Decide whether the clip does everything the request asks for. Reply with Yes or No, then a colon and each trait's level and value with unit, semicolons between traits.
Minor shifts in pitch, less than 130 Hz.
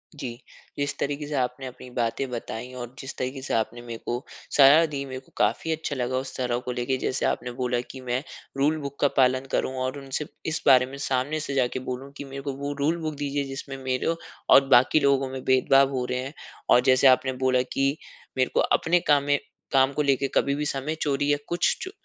No: narrow, 1.8 semitones; low, 135 Hz